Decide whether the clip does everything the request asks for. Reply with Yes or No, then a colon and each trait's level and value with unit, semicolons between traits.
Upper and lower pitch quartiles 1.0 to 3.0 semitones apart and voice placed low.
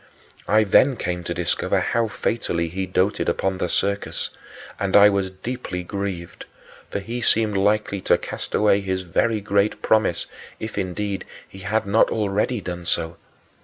Yes: narrow, 2.5 semitones; low, 100 Hz